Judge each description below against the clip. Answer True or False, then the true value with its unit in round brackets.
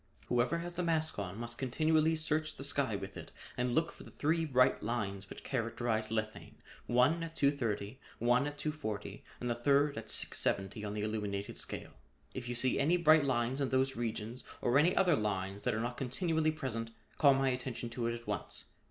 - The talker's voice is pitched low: True (125 Hz)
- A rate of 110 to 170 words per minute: False (195 wpm)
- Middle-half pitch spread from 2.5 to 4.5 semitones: False (5.0 semitones)